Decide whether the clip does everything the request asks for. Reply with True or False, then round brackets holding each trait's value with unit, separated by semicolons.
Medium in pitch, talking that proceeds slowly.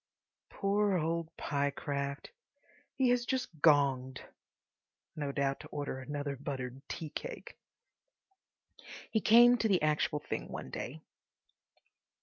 True (150 Hz; 115 wpm)